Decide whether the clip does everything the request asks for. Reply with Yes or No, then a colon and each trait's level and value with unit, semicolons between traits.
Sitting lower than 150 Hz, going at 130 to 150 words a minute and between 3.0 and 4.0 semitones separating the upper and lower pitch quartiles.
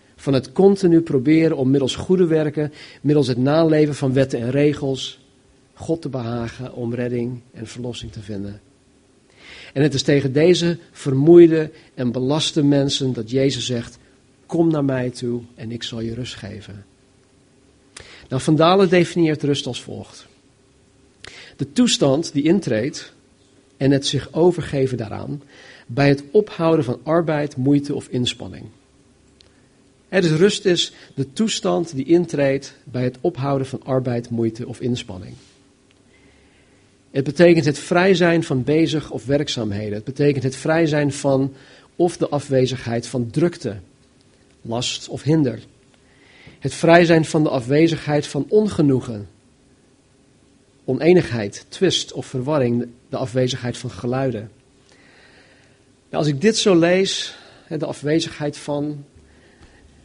Yes: low, 135 Hz; slow, 135 wpm; average, 3.7 semitones